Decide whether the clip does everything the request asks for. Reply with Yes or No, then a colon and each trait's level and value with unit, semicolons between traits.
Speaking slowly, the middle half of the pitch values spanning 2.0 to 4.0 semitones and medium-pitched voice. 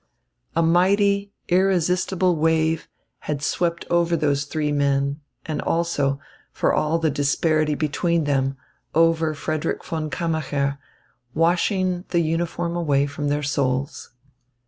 Yes: slow, 120 wpm; average, 2.9 semitones; medium, 160 Hz